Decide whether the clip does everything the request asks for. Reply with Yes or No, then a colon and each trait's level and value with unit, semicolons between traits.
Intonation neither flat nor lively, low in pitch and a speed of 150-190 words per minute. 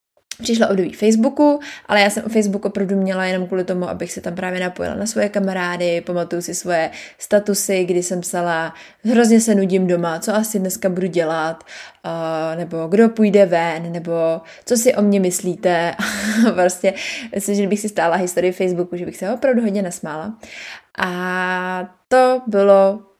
No: average, 3.0 semitones; high, 190 Hz; fast, 170 wpm